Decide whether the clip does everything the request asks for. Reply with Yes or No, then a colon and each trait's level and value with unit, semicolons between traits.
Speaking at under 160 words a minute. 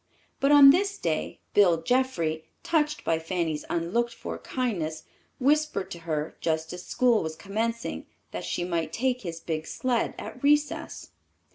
Yes: average, 150 wpm